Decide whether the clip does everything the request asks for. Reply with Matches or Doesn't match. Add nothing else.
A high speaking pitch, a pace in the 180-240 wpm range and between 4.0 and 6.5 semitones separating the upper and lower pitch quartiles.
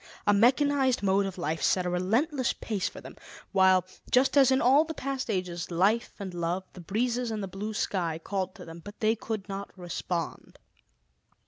Matches